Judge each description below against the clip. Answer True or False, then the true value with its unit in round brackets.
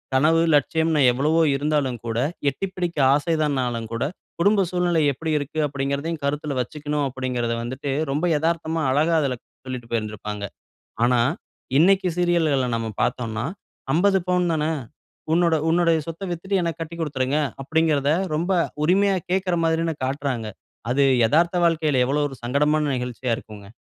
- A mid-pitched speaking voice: True (150 Hz)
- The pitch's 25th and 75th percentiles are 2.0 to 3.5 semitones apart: False (4.3 semitones)